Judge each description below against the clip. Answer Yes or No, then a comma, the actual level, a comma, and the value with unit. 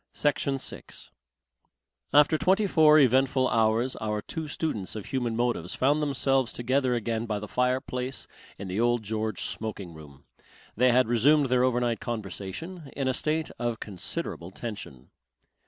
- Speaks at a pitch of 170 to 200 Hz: No, low, 120 Hz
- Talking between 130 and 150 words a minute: Yes, average, 145 wpm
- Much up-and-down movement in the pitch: No, average, 3.9 semitones